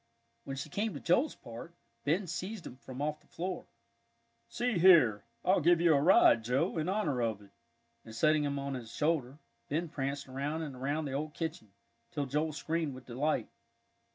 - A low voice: No, medium, 150 Hz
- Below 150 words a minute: No, average, 185 wpm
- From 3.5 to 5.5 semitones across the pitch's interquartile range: Yes, average, 4.1 semitones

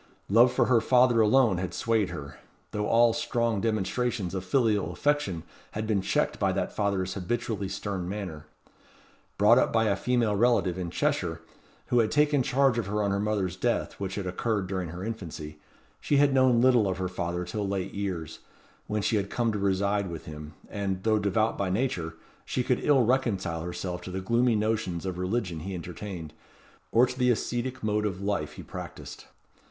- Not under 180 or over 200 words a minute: Yes, average, 190 wpm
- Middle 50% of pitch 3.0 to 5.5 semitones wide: Yes, average, 4.2 semitones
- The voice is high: No, low, 100 Hz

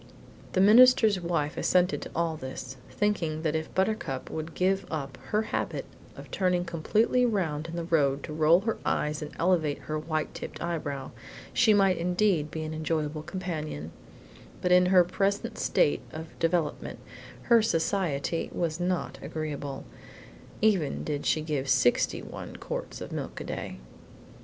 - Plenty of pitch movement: No, average, 3.6 semitones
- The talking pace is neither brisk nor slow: Yes, average, 155 wpm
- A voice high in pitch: No, medium, 165 Hz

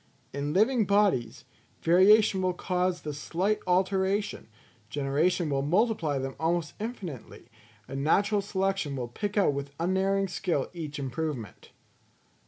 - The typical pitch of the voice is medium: Yes, medium, 175 Hz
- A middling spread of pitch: No, wide, 5.7 semitones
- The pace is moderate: No, slow, 125 wpm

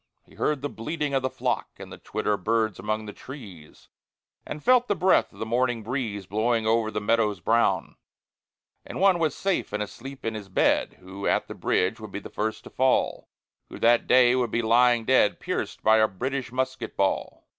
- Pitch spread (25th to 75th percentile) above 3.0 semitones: Yes, average, 3.6 semitones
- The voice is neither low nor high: No, low, 115 Hz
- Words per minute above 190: Yes, average, 200 wpm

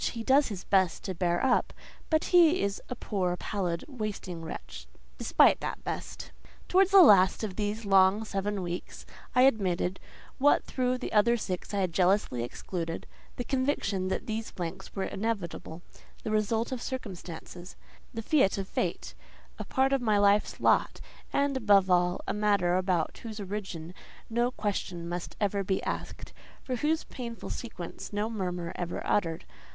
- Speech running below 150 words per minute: No, average, 155 wpm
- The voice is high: Yes, high, 205 Hz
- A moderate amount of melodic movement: Yes, average, 4.4 semitones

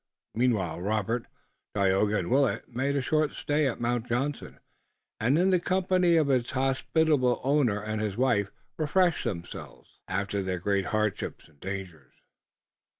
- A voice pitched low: Yes, low, 120 Hz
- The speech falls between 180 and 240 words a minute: No, average, 145 wpm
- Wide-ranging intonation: Yes, wide, 6.0 semitones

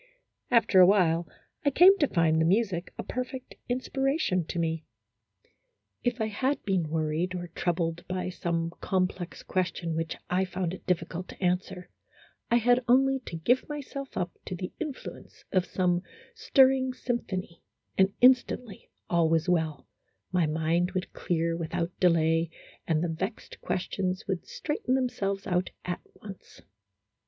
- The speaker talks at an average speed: Yes, average, 150 wpm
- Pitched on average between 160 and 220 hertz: Yes, medium, 185 Hz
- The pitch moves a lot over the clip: Yes, wide, 6.0 semitones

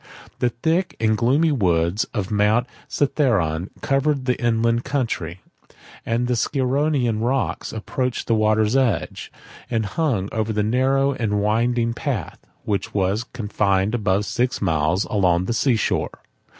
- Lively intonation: No, average, 3.8 semitones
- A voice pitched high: No, low, 115 Hz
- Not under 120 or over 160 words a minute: Yes, slow, 135 wpm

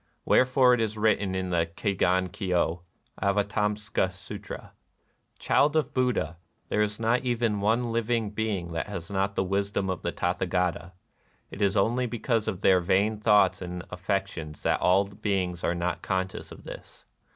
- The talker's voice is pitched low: Yes, low, 100 Hz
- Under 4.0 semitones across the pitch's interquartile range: Yes, average, 3.2 semitones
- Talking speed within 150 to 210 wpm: Yes, average, 165 wpm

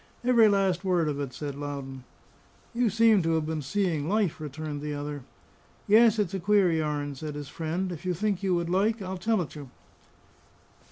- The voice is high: No, medium, 170 Hz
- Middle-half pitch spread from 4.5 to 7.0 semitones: Yes, average, 5.2 semitones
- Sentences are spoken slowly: No, average, 190 wpm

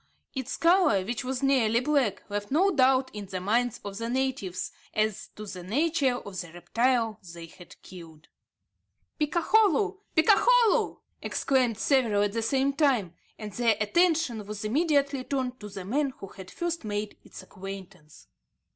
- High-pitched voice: Yes, high, 240 Hz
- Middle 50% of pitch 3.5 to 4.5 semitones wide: No, wide, 5.5 semitones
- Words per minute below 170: Yes, average, 155 wpm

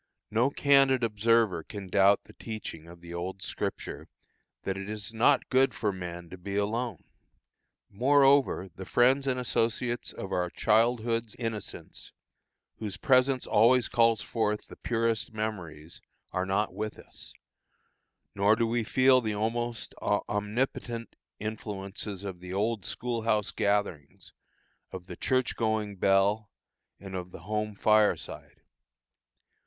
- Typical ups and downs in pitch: Yes, average, 3.3 semitones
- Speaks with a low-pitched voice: Yes, low, 110 Hz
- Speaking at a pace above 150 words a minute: No, slow, 135 wpm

